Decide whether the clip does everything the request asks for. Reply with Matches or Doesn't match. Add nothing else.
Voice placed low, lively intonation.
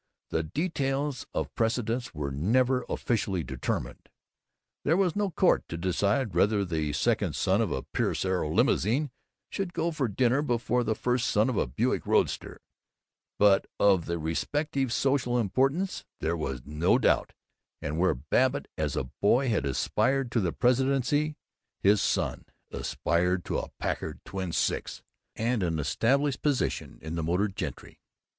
Matches